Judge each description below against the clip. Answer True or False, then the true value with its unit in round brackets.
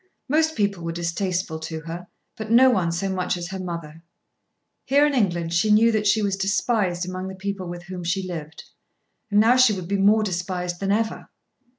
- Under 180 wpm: False (200 wpm)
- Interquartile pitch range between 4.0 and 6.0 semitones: False (3.4 semitones)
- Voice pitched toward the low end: False (190 Hz)